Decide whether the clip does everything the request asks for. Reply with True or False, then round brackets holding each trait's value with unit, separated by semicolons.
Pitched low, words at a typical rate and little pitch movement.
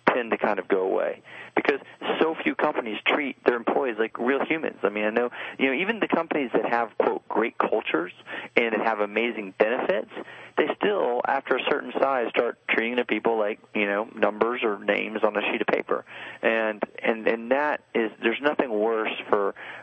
True (110 Hz; 195 wpm; 1.6 semitones)